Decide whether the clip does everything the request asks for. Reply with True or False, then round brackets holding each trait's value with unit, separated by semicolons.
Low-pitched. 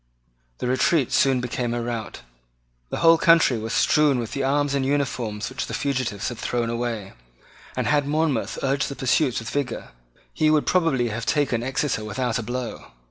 True (130 Hz)